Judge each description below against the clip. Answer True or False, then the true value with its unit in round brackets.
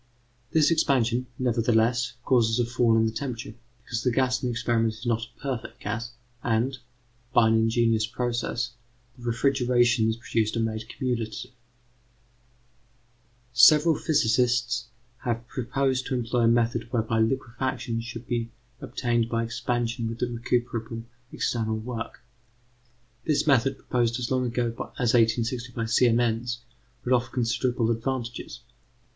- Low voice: True (120 Hz)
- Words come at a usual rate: False (130 wpm)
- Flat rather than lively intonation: True (1.6 semitones)